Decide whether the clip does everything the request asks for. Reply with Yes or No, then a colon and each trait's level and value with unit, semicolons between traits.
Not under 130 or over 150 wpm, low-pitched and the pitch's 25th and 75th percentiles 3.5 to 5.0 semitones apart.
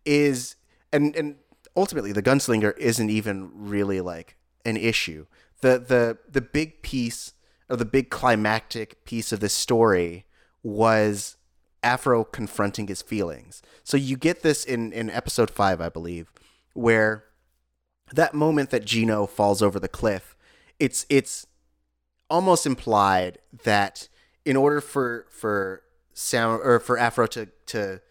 Yes: slow, 135 wpm; low, 115 Hz; average, 4.7 semitones